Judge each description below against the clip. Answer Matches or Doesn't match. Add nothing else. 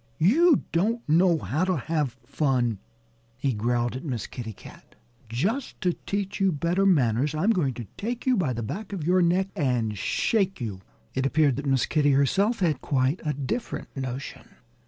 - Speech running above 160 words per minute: Matches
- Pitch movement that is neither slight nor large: Doesn't match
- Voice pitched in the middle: Matches